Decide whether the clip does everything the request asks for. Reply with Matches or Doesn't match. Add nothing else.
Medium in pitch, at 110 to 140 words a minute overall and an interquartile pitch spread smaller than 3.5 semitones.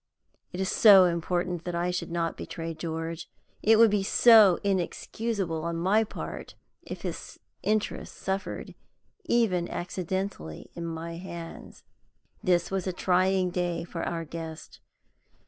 Matches